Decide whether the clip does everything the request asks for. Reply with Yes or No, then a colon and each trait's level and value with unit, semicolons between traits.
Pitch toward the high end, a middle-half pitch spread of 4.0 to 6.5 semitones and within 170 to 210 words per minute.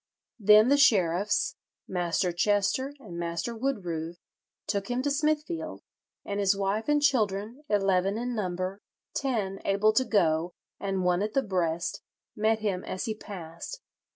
No: high, 200 Hz; average, 4.5 semitones; average, 145 wpm